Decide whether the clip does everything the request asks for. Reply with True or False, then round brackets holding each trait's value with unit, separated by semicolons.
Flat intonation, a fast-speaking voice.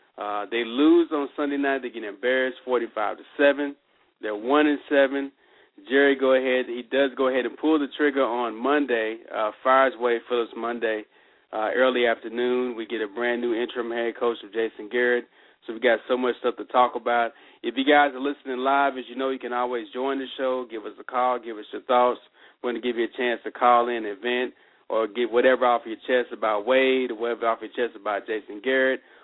True (2.3 semitones; 220 wpm)